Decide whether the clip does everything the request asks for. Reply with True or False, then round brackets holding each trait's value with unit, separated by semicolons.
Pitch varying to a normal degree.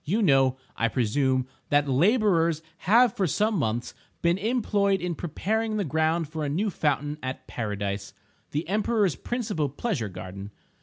False (7.6 semitones)